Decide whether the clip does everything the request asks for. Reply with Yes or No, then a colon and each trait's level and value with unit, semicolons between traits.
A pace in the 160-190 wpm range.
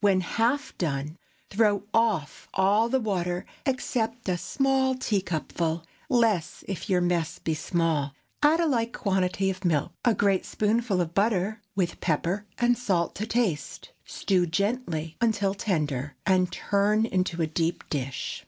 No: average, 145 wpm